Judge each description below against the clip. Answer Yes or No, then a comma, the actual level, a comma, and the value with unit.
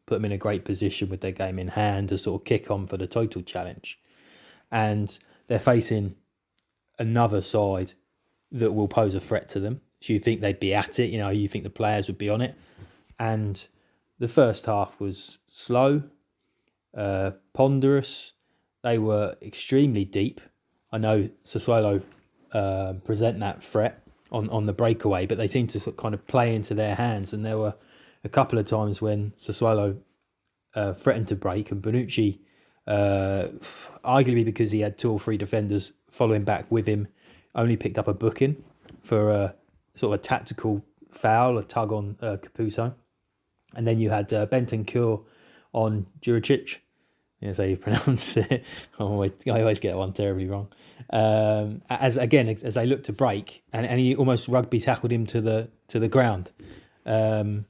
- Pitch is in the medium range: No, low, 110 Hz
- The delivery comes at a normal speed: Yes, average, 180 wpm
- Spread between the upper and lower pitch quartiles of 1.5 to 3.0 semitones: Yes, narrow, 2.5 semitones